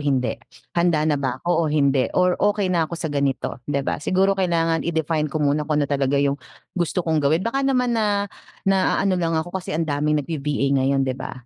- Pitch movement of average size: Yes, average, 4.2 semitones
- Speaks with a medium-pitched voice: Yes, medium, 160 Hz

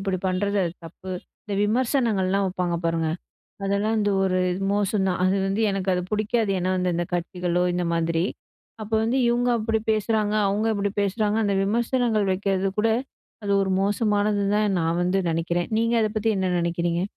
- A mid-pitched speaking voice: No, high, 200 Hz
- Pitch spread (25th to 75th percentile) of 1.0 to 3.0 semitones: Yes, average, 2.7 semitones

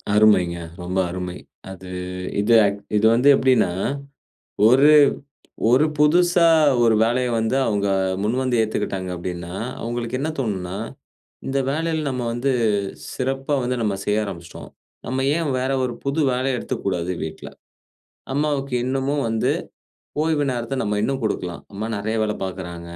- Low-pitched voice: Yes, low, 115 Hz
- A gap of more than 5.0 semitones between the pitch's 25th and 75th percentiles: Yes, wide, 5.5 semitones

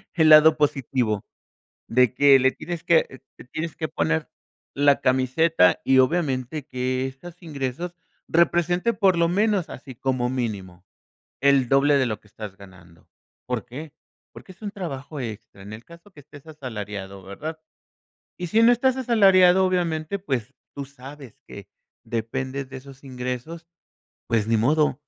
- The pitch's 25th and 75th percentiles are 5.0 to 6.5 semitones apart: Yes, average, 5.3 semitones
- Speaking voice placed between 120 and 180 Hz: Yes, medium, 140 Hz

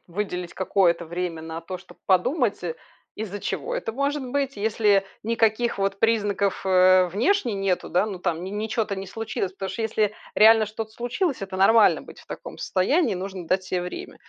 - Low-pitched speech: No, high, 200 Hz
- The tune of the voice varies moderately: Yes, average, 3.3 semitones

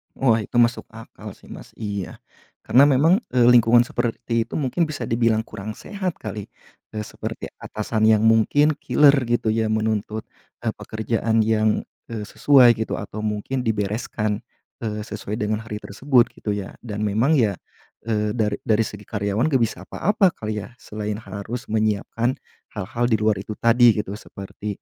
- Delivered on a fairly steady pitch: Yes, narrow, 2.3 semitones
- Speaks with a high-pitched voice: No, low, 110 Hz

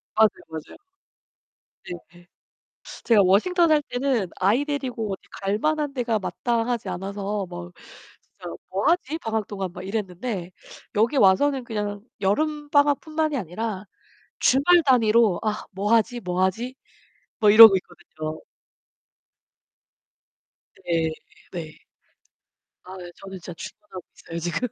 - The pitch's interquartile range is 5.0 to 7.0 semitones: Yes, average, 5.3 semitones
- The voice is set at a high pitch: Yes, high, 215 Hz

